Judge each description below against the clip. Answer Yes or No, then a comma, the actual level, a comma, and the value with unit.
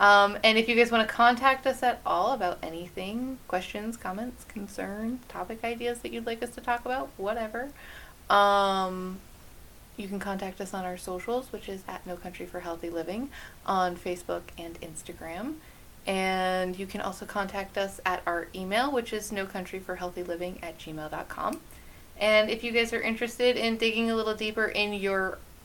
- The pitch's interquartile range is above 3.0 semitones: Yes, average, 4.0 semitones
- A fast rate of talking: No, average, 180 wpm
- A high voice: Yes, high, 200 Hz